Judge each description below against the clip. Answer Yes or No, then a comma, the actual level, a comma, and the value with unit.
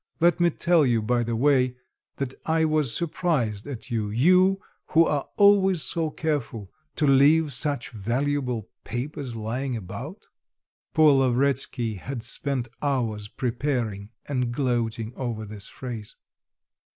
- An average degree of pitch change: Yes, average, 4.5 semitones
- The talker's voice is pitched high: No, low, 130 Hz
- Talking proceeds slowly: Yes, slow, 130 wpm